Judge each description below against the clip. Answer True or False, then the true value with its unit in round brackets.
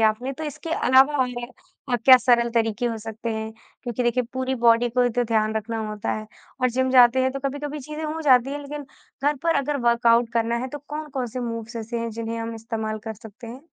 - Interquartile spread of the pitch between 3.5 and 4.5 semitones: False (2.6 semitones)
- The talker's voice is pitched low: False (240 Hz)